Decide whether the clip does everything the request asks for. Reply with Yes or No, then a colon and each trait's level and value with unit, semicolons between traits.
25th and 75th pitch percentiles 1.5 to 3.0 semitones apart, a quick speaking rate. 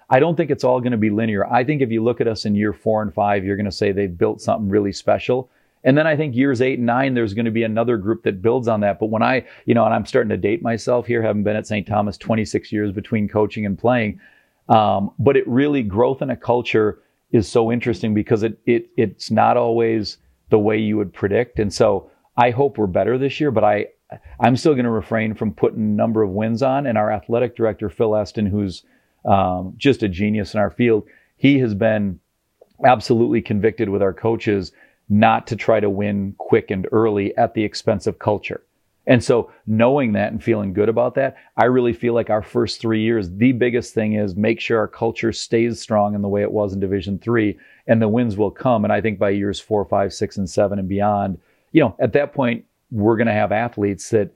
Yes: narrow, 2.4 semitones; fast, 235 wpm